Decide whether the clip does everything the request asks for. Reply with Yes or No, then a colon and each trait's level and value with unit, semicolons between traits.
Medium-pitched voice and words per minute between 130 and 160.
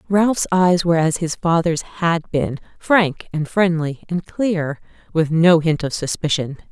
Yes: medium, 165 Hz; average, 150 wpm